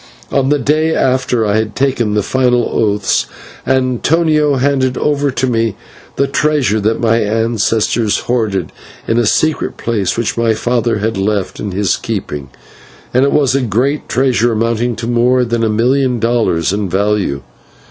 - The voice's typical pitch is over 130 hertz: No, low, 120 Hz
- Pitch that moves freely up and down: No, average, 3.6 semitones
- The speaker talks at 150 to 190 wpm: Yes, average, 160 wpm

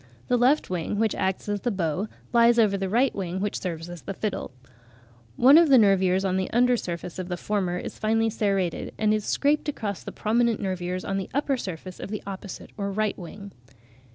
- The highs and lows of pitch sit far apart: No, average, 3.4 semitones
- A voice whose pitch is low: No, high, 200 Hz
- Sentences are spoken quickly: Yes, fast, 210 wpm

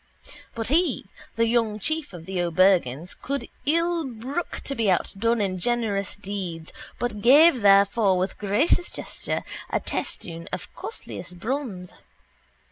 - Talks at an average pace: No, slow, 130 wpm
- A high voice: Yes, high, 210 Hz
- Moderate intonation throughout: No, wide, 5.9 semitones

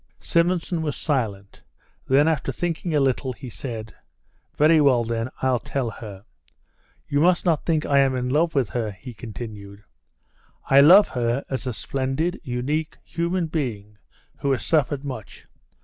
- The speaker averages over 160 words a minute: No, average, 155 wpm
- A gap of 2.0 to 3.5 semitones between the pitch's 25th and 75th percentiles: No, average, 4.9 semitones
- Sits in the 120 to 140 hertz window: Yes, low, 135 Hz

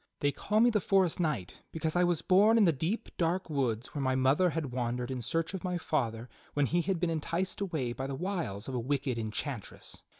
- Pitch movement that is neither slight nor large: No, wide, 5.7 semitones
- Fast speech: Yes, fast, 225 wpm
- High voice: No, medium, 155 Hz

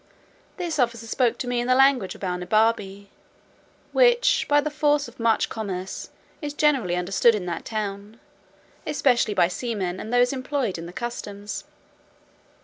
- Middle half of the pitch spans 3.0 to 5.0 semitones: No, wide, 5.5 semitones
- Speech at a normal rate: Yes, average, 150 wpm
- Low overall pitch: No, high, 230 Hz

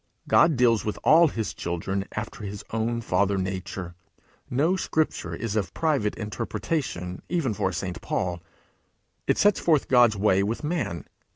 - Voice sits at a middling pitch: No, low, 105 Hz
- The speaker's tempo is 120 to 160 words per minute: Yes, average, 155 wpm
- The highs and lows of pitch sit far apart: Yes, wide, 6.3 semitones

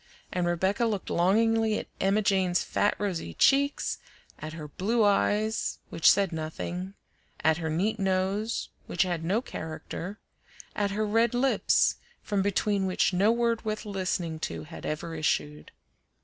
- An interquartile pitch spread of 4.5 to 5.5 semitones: No, average, 4.0 semitones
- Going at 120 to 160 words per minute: Yes, average, 150 wpm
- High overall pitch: Yes, high, 195 Hz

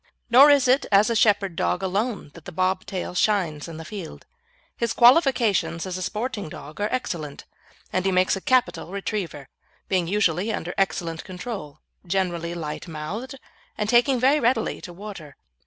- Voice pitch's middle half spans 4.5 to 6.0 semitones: Yes, average, 5.0 semitones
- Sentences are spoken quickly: No, average, 170 wpm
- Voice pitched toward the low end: No, high, 195 Hz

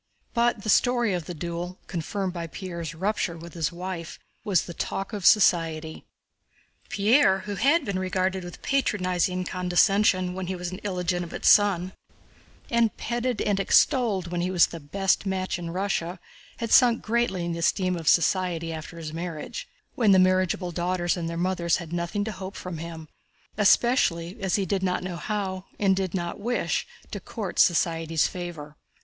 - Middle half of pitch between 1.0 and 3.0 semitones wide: Yes, average, 2.7 semitones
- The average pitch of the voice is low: No, medium, 185 Hz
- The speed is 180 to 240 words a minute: No, average, 165 wpm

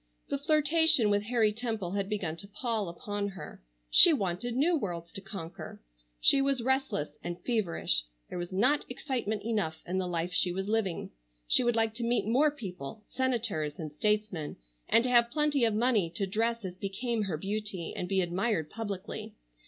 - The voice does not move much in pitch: No, average, 5.0 semitones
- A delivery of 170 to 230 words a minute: Yes, average, 175 wpm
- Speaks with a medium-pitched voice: No, high, 210 Hz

